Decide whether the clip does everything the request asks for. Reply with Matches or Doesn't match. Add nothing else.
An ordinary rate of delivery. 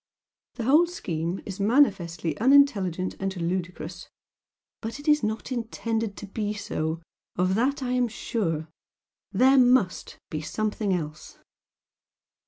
Doesn't match